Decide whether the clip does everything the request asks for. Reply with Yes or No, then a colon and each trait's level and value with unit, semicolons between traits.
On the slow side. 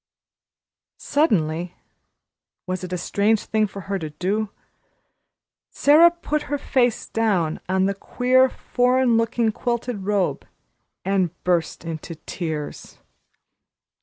Yes: slow, 110 wpm